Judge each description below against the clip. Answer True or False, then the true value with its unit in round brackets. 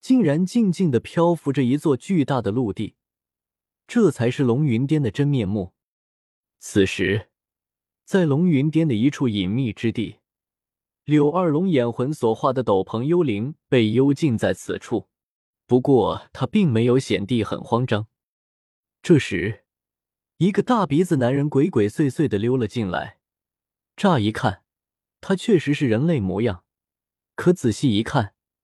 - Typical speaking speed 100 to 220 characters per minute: True (210 characters per minute)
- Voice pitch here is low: True (130 Hz)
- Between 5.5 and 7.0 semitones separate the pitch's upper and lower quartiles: True (6.2 semitones)